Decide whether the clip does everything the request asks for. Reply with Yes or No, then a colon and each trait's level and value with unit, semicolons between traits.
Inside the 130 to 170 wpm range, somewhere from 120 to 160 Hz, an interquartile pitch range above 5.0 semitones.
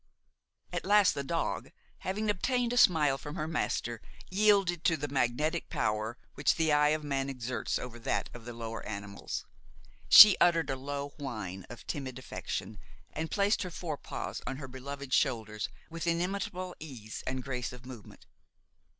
Yes: average, 165 wpm; medium, 140 Hz; wide, 5.4 semitones